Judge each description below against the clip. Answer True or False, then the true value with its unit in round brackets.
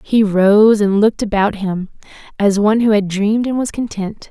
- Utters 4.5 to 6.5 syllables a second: True (5.1 syllables/s)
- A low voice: False (210 Hz)